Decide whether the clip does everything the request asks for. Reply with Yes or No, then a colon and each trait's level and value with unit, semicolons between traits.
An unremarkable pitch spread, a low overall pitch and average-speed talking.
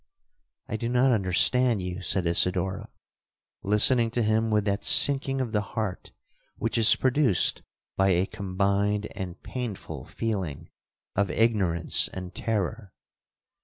No: average, 3.5 semitones; low, 105 Hz; slow, 130 wpm